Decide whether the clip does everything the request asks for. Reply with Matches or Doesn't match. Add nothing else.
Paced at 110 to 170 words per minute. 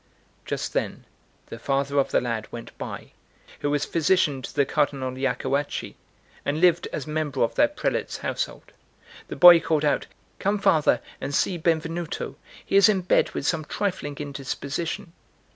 Matches